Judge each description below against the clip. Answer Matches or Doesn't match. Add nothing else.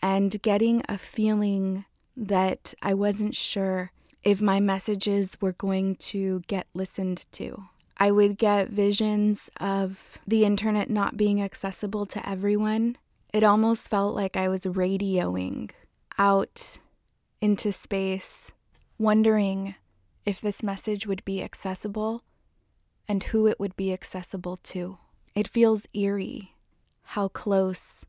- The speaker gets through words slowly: Matches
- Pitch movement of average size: Doesn't match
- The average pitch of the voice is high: Matches